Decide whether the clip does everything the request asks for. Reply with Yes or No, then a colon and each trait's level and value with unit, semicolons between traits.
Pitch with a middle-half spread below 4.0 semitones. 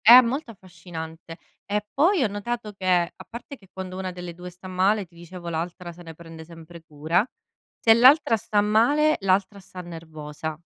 No: average, 4.3 semitones